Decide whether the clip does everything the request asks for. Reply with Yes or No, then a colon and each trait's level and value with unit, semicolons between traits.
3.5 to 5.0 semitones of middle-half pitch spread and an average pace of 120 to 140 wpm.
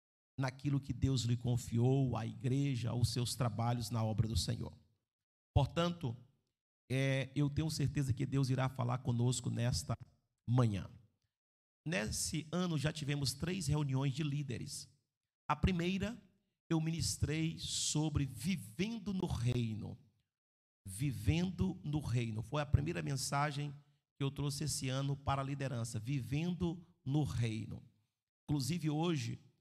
Yes: average, 3.9 semitones; average, 125 wpm